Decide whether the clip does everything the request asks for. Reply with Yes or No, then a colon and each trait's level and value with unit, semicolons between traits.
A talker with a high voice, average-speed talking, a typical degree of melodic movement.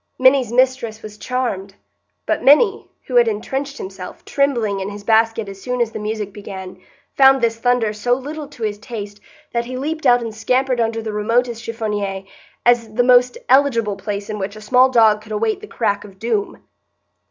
Yes: high, 230 Hz; average, 185 wpm; average, 3.2 semitones